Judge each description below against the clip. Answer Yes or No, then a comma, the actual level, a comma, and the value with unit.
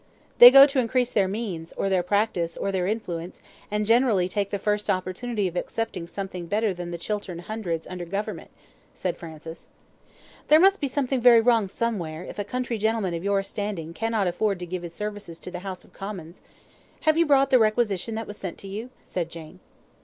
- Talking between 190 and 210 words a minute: Yes, average, 200 wpm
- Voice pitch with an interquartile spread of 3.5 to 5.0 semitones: Yes, average, 4.2 semitones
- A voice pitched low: No, high, 200 Hz